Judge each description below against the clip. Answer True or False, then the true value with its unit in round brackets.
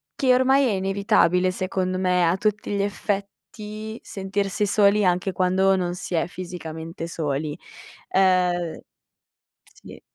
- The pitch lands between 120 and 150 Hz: False (190 Hz)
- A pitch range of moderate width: False (2.3 semitones)